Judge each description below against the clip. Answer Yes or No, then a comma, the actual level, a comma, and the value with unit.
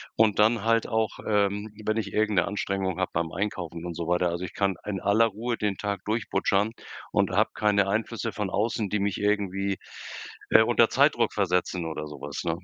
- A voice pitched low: Yes, low, 100 Hz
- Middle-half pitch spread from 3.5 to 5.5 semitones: No, narrow, 2.5 semitones